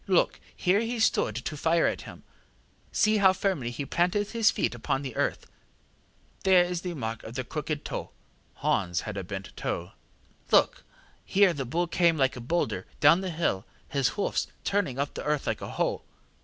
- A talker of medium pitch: Yes, medium, 160 Hz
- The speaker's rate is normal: Yes, average, 185 wpm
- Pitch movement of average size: No, wide, 6.9 semitones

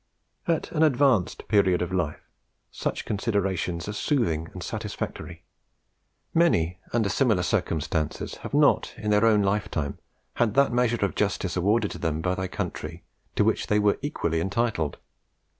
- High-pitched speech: No, low, 100 Hz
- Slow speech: No, average, 150 wpm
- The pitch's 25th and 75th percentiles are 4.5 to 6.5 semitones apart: Yes, average, 5.0 semitones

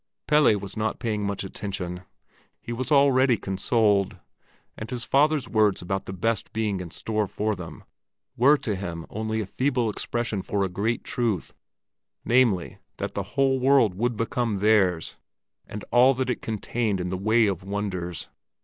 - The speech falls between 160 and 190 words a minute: Yes, average, 165 wpm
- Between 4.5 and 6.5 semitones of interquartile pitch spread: No, average, 3.8 semitones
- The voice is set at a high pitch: No, low, 110 Hz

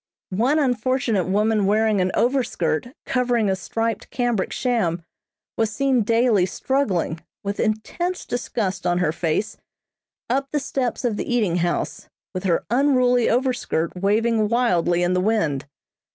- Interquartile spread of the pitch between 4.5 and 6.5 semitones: Yes, average, 5.2 semitones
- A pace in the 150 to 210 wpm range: No, average, 140 wpm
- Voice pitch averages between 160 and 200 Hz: No, high, 220 Hz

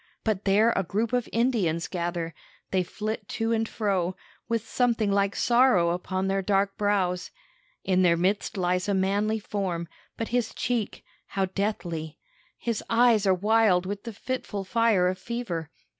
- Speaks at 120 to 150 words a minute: No, average, 160 wpm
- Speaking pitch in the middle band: No, high, 200 Hz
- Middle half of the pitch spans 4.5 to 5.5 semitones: No, average, 3.6 semitones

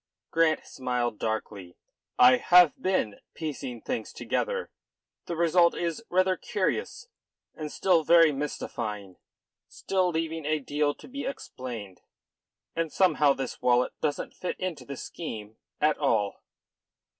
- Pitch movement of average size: No, wide, 5.8 semitones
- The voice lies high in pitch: No, medium, 150 Hz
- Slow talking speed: Yes, slow, 125 wpm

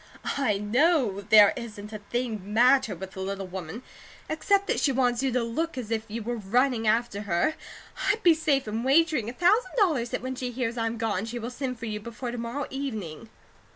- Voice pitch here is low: No, high, 235 Hz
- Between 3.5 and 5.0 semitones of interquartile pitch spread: Yes, average, 3.8 semitones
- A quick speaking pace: Yes, fast, 215 wpm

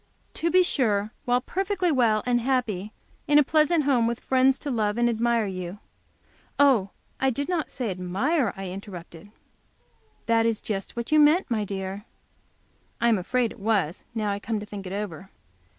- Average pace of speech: Yes, average, 180 wpm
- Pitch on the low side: No, high, 230 Hz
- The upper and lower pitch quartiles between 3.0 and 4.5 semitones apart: No, average, 4.9 semitones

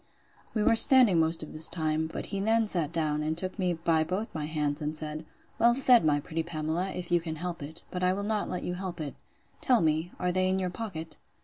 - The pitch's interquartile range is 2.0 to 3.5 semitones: Yes, average, 3.2 semitones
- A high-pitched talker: No, medium, 170 Hz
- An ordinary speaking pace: No, fast, 240 wpm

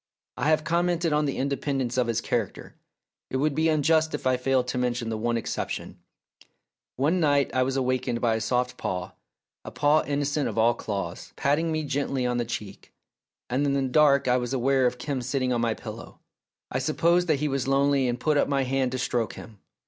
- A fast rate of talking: Yes, fast, 210 wpm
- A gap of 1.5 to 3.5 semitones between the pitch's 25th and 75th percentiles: Yes, average, 3.0 semitones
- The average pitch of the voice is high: No, low, 135 Hz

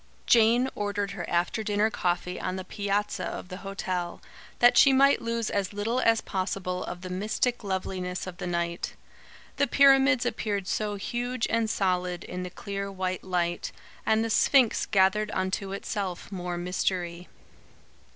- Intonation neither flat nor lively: Yes, average, 3.4 semitones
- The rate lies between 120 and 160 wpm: Yes, average, 155 wpm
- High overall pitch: Yes, high, 195 Hz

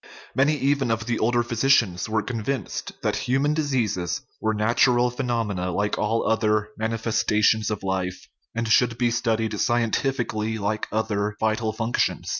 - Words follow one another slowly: No, average, 145 wpm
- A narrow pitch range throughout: Yes, narrow, 2.2 semitones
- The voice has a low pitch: Yes, low, 115 Hz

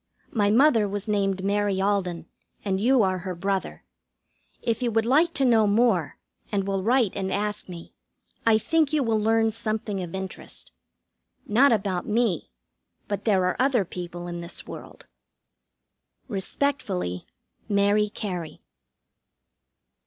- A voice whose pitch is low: No, high, 205 Hz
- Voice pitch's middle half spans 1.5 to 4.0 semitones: Yes, average, 3.1 semitones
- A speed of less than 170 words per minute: Yes, average, 140 wpm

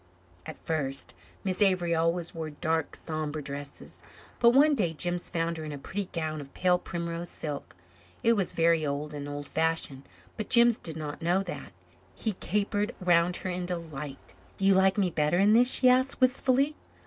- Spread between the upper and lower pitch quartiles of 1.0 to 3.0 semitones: No, average, 4.1 semitones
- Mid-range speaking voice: Yes, medium, 170 Hz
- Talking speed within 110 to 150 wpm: No, average, 180 wpm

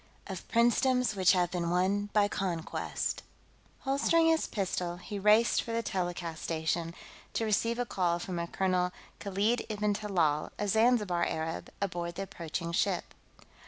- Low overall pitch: No, high, 190 Hz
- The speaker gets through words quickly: No, average, 150 wpm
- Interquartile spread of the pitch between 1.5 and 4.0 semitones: Yes, average, 3.7 semitones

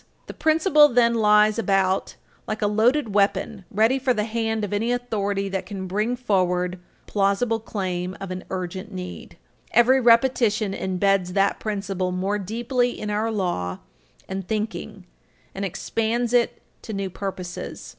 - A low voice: No, high, 210 Hz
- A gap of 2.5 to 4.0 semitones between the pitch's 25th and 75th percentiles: Yes, average, 3.3 semitones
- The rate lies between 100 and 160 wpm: Yes, average, 150 wpm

